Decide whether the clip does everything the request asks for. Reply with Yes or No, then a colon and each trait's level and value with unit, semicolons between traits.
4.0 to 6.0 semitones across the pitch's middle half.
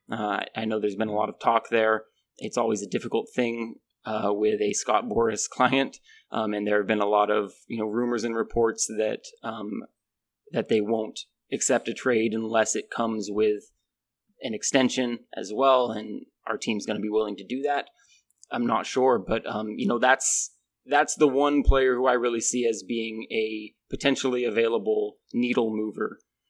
No: average, 2.8 semitones